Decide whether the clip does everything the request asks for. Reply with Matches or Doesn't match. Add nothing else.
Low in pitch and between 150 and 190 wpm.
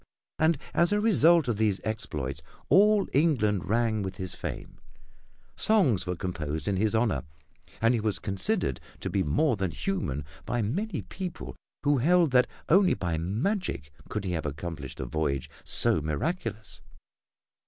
Matches